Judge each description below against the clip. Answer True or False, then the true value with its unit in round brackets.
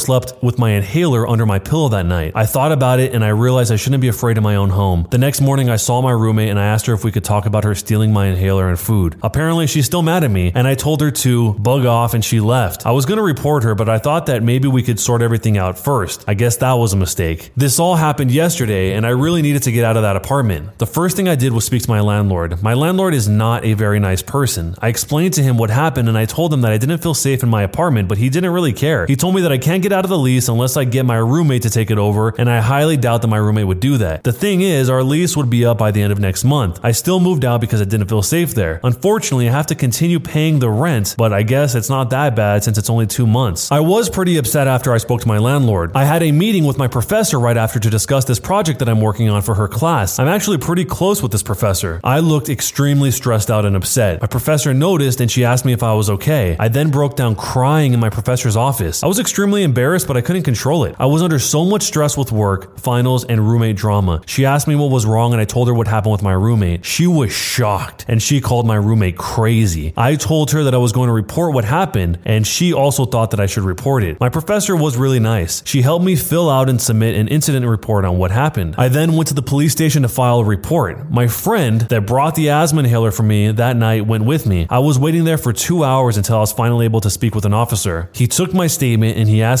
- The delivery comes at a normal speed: False (275 wpm)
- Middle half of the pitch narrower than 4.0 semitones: False (5.0 semitones)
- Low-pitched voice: True (125 Hz)